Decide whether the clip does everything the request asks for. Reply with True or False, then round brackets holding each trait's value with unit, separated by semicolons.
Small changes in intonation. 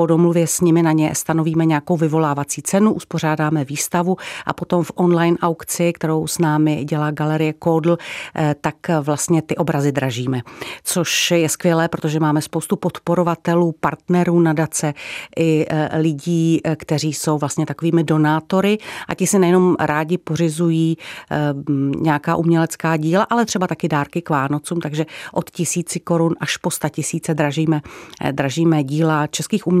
True (1.9 semitones)